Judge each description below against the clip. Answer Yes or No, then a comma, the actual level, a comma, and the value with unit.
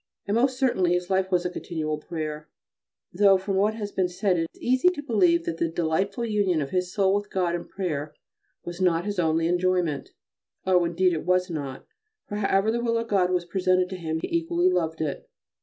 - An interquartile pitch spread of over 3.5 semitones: No, average, 2.9 semitones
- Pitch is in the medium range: Yes, medium, 180 Hz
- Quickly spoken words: Yes, fast, 210 wpm